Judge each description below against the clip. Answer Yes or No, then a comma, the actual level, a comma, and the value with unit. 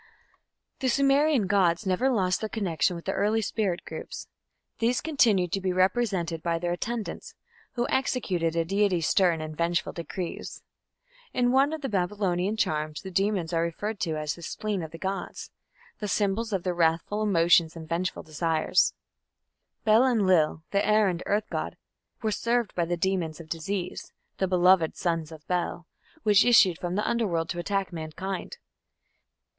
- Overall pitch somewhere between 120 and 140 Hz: No, medium, 185 Hz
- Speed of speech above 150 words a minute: Yes, average, 165 wpm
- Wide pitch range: No, average, 4.1 semitones